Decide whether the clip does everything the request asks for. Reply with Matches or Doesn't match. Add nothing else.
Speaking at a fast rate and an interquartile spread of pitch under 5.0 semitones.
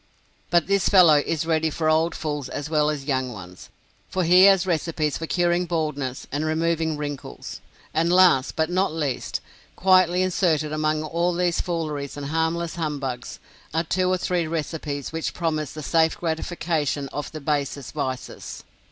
Doesn't match